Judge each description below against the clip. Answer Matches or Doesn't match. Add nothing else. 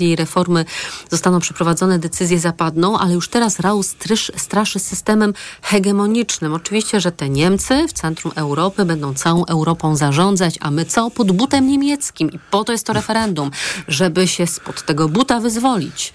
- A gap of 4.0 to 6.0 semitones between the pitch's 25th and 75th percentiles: Matches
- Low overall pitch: Doesn't match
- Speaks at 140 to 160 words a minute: Matches